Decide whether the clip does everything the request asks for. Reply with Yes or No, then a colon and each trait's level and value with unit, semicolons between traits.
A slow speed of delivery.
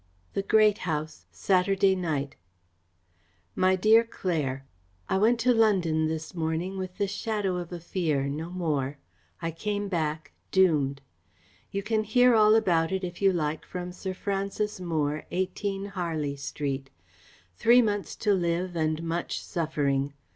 No: average, 145 wpm